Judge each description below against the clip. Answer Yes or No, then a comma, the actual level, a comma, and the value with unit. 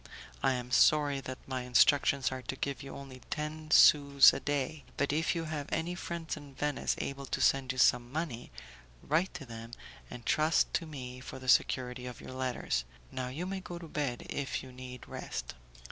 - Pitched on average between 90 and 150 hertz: Yes, medium, 140 Hz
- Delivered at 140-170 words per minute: No, average, 195 wpm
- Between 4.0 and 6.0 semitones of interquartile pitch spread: No, average, 3.2 semitones